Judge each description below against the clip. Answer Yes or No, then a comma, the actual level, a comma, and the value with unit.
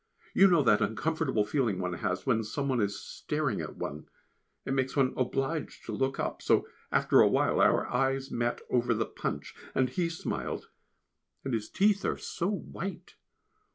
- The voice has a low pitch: Yes, low, 130 Hz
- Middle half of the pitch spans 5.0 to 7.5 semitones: Yes, average, 5.3 semitones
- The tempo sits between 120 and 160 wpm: No, average, 175 wpm